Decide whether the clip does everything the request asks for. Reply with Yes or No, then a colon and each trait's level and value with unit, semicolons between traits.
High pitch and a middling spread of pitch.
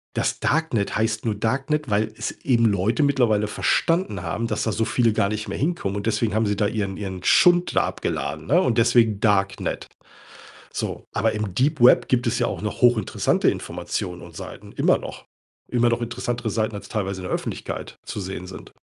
No: low, 110 Hz; average, 3.0 semitones